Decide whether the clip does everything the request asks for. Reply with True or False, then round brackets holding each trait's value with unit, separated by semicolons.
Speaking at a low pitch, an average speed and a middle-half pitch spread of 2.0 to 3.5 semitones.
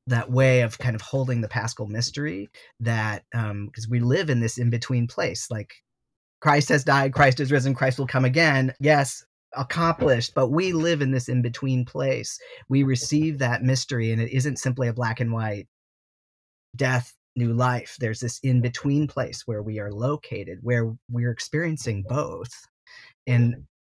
True (125 Hz; 175 wpm; 2.8 semitones)